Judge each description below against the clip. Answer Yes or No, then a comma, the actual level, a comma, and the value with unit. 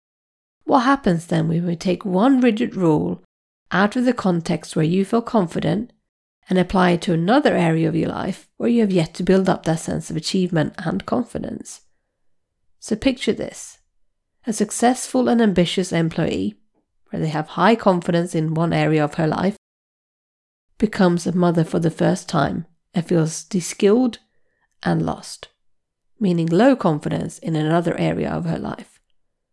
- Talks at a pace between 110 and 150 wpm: No, average, 160 wpm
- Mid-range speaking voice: Yes, medium, 180 Hz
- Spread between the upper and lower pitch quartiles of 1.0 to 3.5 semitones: No, average, 4.8 semitones